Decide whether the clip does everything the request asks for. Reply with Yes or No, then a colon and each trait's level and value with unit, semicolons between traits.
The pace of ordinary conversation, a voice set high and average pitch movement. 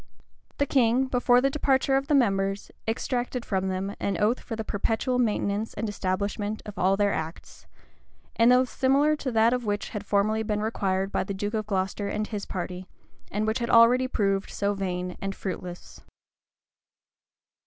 Yes: average, 170 wpm; high, 210 Hz; average, 3.8 semitones